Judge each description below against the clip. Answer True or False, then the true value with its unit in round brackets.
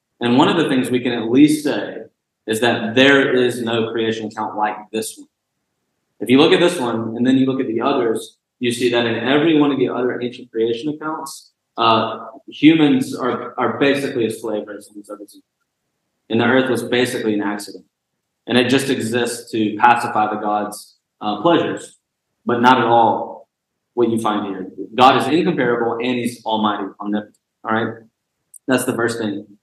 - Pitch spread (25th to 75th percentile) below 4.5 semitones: True (2.7 semitones)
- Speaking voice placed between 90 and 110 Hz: False (120 Hz)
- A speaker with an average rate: True (185 wpm)